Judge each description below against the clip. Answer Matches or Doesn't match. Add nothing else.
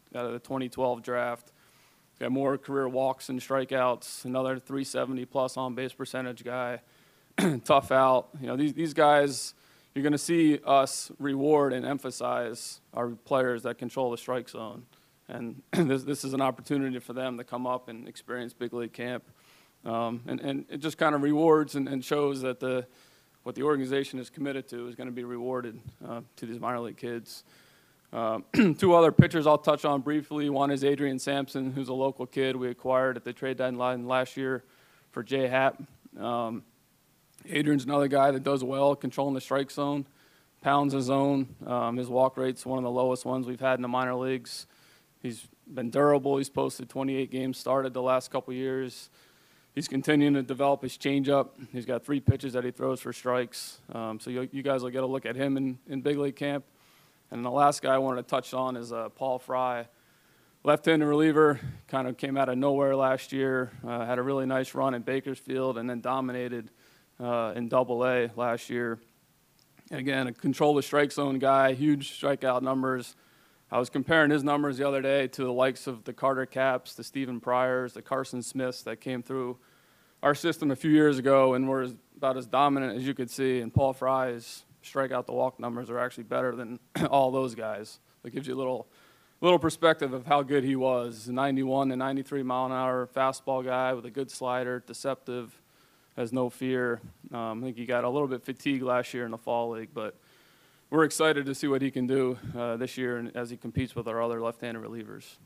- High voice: Doesn't match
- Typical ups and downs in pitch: Doesn't match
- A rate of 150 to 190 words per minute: Doesn't match